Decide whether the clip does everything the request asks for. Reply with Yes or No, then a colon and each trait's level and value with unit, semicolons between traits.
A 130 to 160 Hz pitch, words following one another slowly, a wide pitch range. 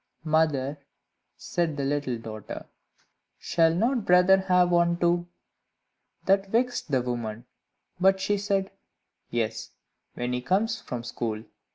No: medium, 170 Hz; slow, 125 wpm; wide, 7.4 semitones